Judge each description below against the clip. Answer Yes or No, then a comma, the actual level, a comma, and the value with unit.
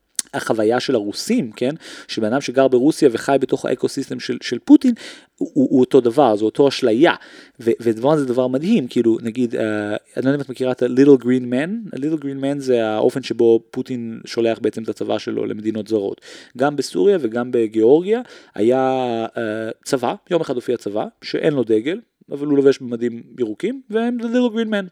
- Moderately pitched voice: No, low, 130 Hz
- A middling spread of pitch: No, wide, 6.2 semitones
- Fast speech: Yes, fast, 180 wpm